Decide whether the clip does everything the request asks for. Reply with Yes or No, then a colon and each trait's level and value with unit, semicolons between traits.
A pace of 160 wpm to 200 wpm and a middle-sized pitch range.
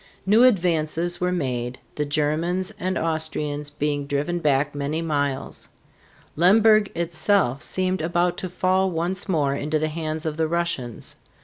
No: average, 140 wpm; average, 3.5 semitones